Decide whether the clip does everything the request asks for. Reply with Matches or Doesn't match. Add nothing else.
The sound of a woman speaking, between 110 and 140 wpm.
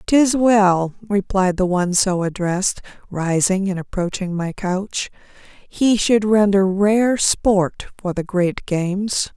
Matches